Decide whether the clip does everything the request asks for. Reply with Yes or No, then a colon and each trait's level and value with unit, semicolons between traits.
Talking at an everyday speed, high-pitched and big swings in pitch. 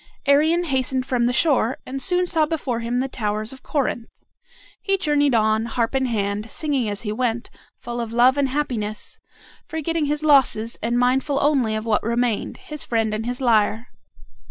No: average, 180 wpm; very high, 250 Hz; average, 4.0 semitones